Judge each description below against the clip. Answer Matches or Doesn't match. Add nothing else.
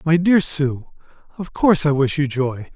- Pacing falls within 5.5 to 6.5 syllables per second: Doesn't match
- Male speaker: Matches